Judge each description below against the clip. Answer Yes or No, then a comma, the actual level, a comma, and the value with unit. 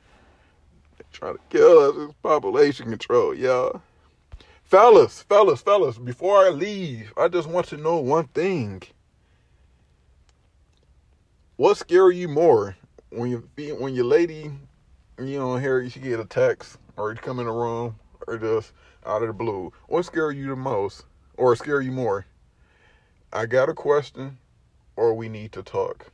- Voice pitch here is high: No, low, 130 Hz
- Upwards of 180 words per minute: No, average, 155 wpm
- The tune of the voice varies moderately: No, wide, 8.1 semitones